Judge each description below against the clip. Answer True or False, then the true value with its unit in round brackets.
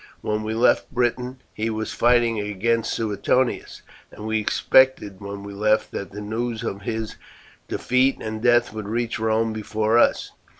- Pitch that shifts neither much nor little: False (2.1 semitones)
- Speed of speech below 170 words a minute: True (160 wpm)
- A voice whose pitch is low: True (110 Hz)